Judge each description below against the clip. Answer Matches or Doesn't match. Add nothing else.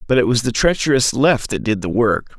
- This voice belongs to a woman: Doesn't match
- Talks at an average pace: Doesn't match